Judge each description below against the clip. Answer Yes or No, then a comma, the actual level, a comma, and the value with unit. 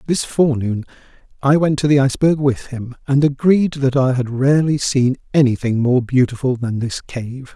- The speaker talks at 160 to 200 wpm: Yes, average, 185 wpm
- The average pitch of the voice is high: No, low, 135 Hz